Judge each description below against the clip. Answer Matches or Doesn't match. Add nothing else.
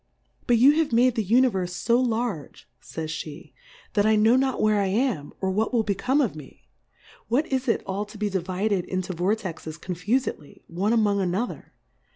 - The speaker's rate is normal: Matches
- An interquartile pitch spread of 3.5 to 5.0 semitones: Matches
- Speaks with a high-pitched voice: Matches